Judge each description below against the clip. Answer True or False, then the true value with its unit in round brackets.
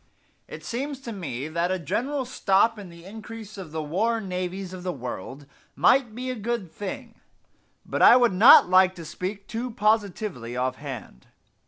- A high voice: True (195 Hz)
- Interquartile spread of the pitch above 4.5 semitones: True (5.2 semitones)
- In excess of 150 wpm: True (170 wpm)